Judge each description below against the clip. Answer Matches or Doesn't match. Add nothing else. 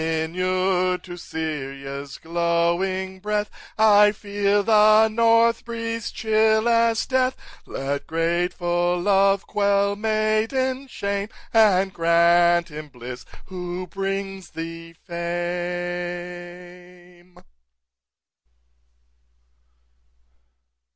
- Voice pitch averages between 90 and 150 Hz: Doesn't match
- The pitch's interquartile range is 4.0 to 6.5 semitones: Doesn't match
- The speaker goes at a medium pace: Doesn't match